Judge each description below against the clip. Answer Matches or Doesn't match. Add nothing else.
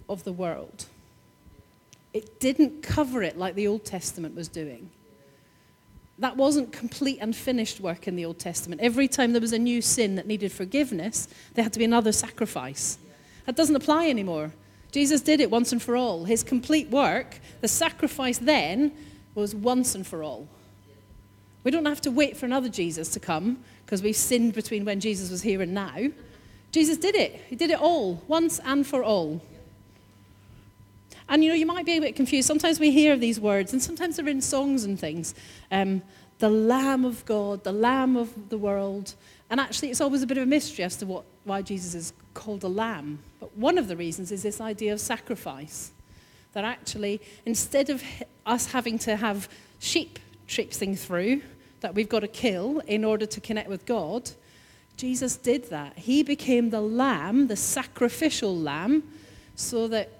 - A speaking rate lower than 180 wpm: Doesn't match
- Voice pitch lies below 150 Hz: Doesn't match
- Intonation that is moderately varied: Doesn't match